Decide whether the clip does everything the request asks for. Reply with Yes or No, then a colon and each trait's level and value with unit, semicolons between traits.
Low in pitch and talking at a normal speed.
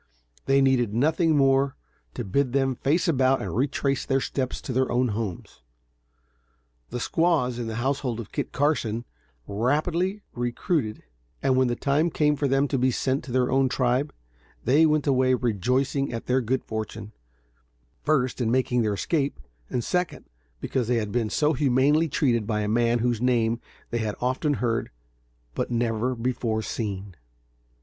Yes: low, 130 Hz; average, 165 wpm